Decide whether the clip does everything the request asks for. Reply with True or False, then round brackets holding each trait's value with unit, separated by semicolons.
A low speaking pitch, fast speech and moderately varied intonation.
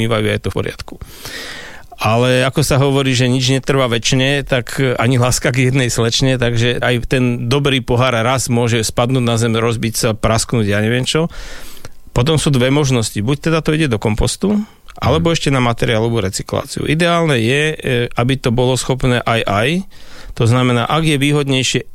True (125 Hz; 170 wpm; 3.0 semitones)